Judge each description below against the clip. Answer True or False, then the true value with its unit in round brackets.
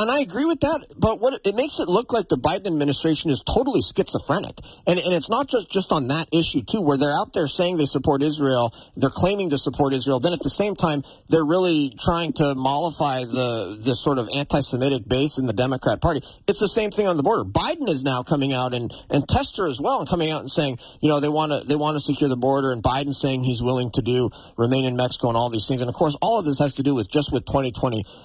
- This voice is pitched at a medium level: True (145 Hz)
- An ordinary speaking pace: False (255 wpm)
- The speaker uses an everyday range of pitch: True (4.4 semitones)